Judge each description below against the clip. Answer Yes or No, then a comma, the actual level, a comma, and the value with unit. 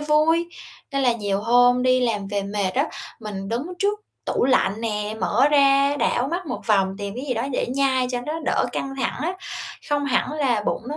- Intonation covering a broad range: No, average, 5.0 semitones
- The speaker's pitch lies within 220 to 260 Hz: Yes, very high, 250 Hz